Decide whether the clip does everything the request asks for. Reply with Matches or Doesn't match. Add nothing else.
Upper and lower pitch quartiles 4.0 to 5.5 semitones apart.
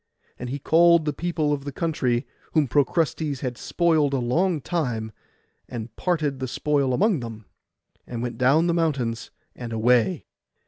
Matches